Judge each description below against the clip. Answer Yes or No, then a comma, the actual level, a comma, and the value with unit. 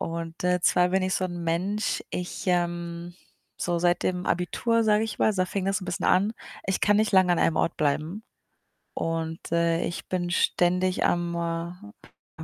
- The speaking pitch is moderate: Yes, medium, 180 Hz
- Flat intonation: Yes, narrow, 1.8 semitones